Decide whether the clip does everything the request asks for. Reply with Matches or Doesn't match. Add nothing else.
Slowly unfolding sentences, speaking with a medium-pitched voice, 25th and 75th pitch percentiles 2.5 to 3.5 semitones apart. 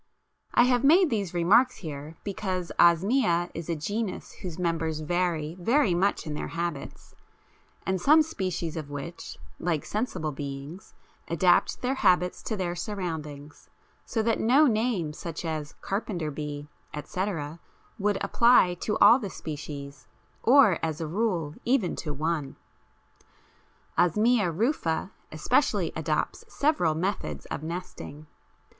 Doesn't match